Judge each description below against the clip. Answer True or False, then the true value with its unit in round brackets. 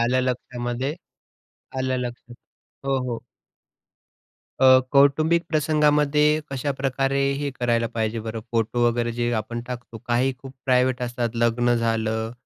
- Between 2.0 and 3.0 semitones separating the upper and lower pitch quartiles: True (2.4 semitones)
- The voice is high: False (125 Hz)